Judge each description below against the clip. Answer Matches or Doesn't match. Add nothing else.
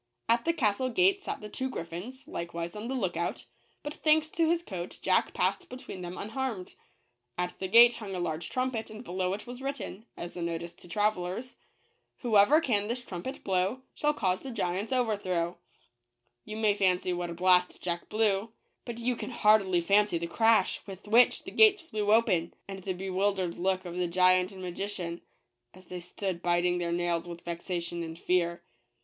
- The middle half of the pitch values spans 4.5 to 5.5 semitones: Matches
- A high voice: Matches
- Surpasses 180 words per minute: Matches